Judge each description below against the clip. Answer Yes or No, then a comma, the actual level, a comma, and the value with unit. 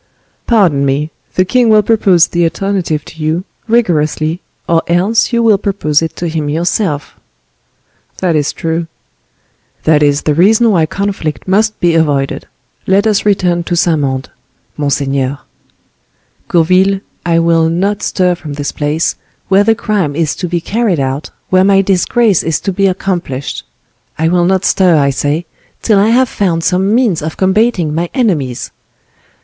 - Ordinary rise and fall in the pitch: Yes, average, 4.2 semitones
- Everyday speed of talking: Yes, average, 155 wpm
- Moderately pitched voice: Yes, medium, 175 Hz